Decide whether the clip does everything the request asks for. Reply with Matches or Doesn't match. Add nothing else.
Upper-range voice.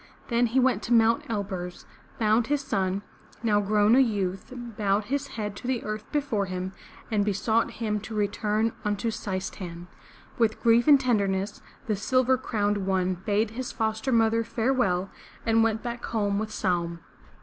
Matches